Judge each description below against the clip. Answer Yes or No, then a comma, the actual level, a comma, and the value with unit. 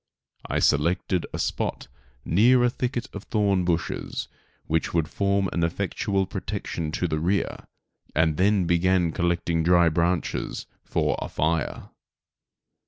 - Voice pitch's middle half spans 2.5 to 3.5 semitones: Yes, average, 2.9 semitones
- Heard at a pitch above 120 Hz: No, very low, 90 Hz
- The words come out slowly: Yes, slow, 130 wpm